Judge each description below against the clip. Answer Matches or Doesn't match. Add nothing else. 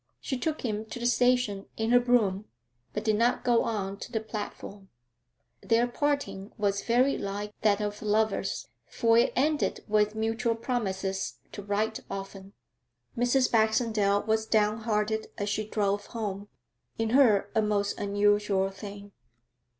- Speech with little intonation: Matches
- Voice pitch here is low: Doesn't match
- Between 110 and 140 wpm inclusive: Doesn't match